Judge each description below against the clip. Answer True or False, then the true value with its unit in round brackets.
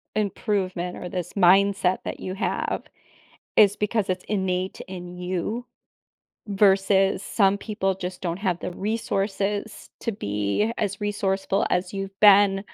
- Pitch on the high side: True (195 Hz)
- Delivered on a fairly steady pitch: True (1.9 semitones)